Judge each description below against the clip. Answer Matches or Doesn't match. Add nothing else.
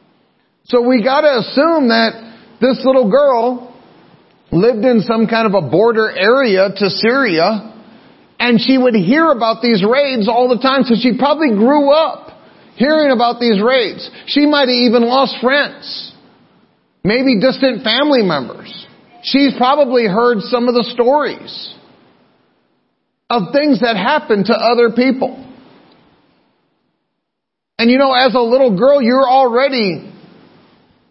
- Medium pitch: Doesn't match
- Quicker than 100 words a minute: Matches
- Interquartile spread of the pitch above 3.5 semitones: Doesn't match